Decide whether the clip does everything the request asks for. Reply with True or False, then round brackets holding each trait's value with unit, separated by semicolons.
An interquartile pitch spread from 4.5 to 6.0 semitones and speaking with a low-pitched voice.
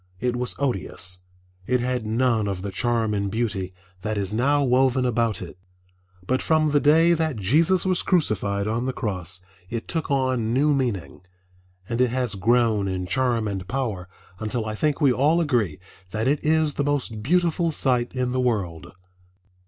True (4.9 semitones; 120 Hz)